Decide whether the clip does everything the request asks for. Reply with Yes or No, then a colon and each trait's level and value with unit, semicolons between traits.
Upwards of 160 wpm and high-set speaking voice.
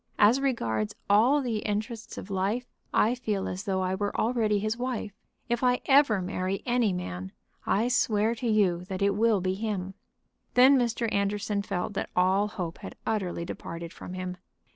Yes: average, 175 wpm; high, 205 Hz